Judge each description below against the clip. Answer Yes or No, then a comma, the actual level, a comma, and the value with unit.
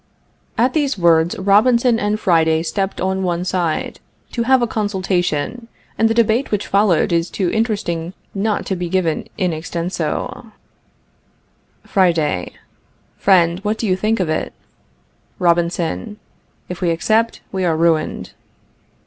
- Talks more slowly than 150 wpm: Yes, slow, 135 wpm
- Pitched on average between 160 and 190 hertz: Yes, medium, 185 Hz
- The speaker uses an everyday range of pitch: Yes, average, 4.1 semitones